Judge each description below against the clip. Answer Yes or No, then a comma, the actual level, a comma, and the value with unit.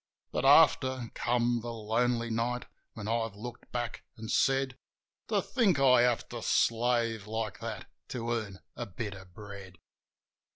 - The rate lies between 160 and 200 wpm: No, average, 150 wpm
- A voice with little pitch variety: Yes, narrow, 2.1 semitones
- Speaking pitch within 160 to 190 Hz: No, low, 115 Hz